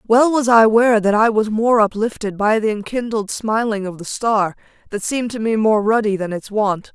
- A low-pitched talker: No, high, 215 Hz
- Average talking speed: No, fast, 215 wpm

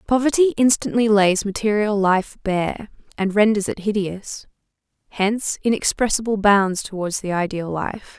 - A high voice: Yes, high, 205 Hz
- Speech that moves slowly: Yes, slow, 125 wpm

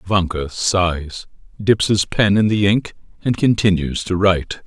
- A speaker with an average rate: Yes, average, 155 wpm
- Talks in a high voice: No, very low, 95 Hz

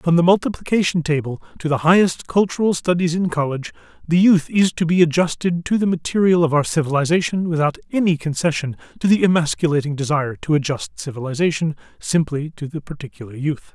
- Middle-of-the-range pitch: Yes, medium, 160 Hz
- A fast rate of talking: No, average, 165 wpm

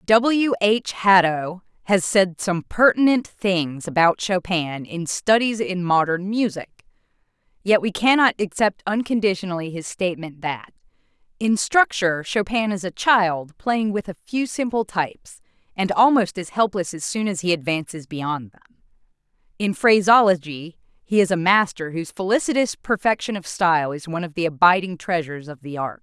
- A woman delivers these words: Yes, female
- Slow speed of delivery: No, average, 150 wpm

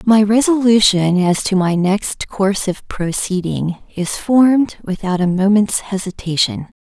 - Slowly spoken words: Yes, slow, 130 wpm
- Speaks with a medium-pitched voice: No, high, 200 Hz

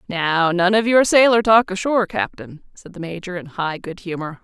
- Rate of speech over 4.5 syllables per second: Yes, 5.0 syllables/s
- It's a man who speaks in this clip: No, female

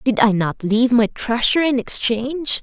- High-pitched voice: Yes, high, 240 Hz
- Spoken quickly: No, average, 185 wpm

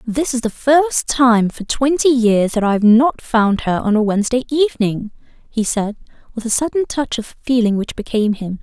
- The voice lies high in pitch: Yes, high, 235 Hz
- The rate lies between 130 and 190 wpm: No, average, 200 wpm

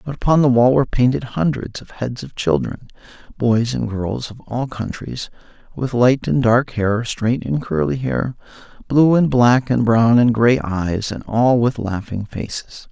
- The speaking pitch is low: Yes, low, 120 Hz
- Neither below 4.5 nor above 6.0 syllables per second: No, 4.3 syllables/s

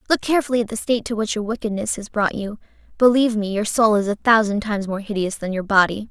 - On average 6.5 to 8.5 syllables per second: Yes, 6.7 syllables/s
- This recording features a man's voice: No, female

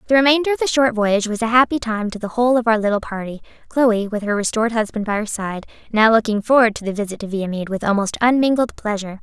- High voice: Yes, high, 220 Hz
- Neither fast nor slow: No, fast, 240 wpm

